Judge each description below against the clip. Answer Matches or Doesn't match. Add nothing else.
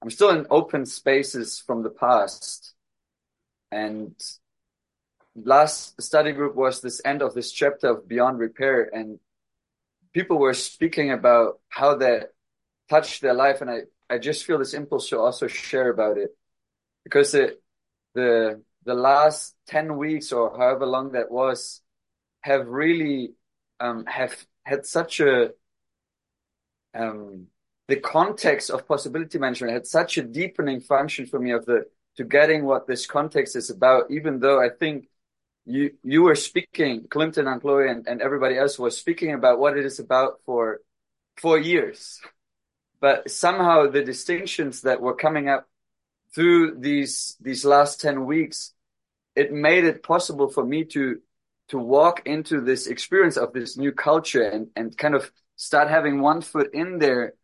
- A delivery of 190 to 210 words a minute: Doesn't match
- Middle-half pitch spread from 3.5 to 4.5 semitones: Matches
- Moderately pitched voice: Matches